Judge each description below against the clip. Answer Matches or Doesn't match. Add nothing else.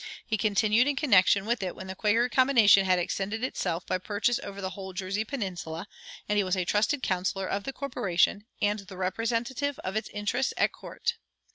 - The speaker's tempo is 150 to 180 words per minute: Doesn't match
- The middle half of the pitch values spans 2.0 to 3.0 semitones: Doesn't match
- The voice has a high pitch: Matches